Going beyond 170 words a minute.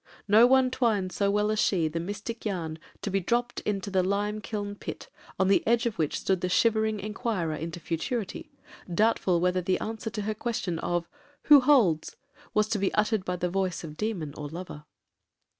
Yes: average, 190 wpm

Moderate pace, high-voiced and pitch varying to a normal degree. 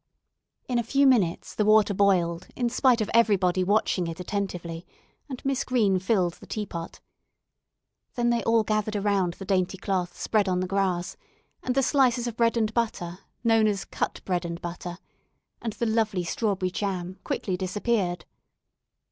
Yes: average, 165 wpm; high, 200 Hz; average, 4.1 semitones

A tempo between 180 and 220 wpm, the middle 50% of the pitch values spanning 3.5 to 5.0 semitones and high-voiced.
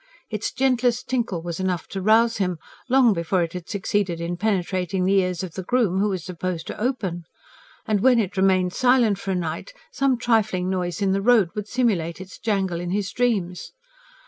Yes: average, 195 wpm; average, 4.1 semitones; high, 195 Hz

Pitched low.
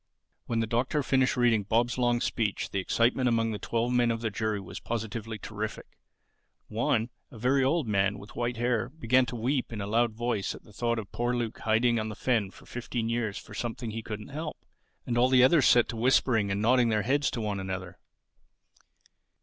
Yes: low, 115 Hz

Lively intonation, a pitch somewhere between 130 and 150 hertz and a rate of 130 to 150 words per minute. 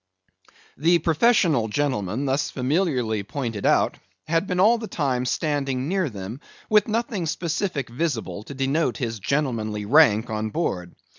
Yes: wide, 6.7 semitones; medium, 140 Hz; average, 140 wpm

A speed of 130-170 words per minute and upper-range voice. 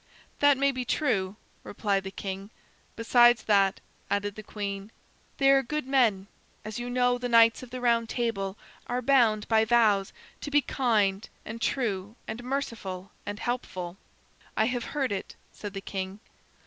Yes: average, 160 wpm; high, 225 Hz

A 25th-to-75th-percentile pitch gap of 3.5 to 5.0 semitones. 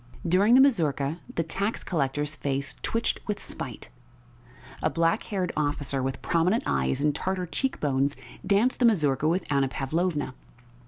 No: wide, 5.5 semitones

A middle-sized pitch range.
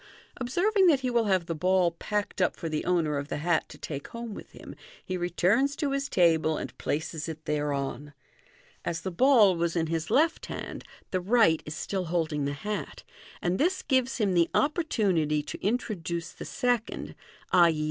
No: wide, 6.6 semitones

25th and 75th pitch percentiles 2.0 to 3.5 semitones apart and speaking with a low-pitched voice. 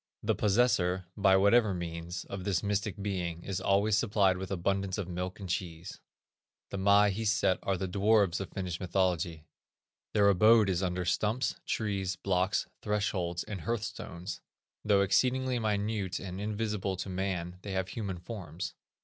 Yes: narrow, 2.4 semitones; very low, 95 Hz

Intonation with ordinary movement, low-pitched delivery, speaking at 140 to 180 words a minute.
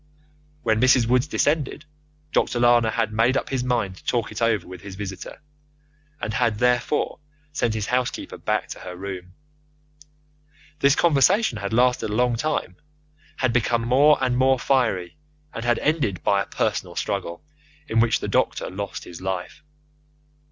Yes: average, 4.0 semitones; low, 120 Hz; average, 160 wpm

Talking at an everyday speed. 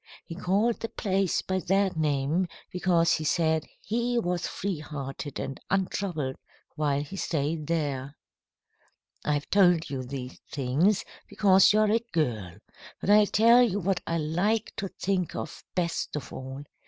Yes: average, 155 wpm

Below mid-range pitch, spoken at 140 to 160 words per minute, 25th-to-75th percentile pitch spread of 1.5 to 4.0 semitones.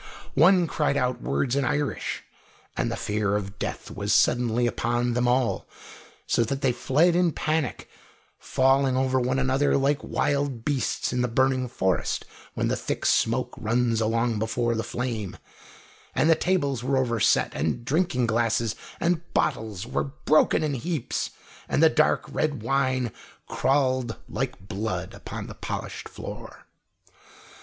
Yes: low, 130 Hz; average, 150 wpm; average, 3.3 semitones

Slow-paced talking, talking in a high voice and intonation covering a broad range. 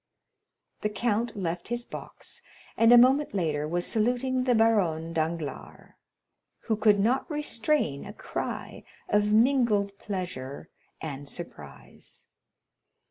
Yes: slow, 115 wpm; high, 210 Hz; wide, 6.2 semitones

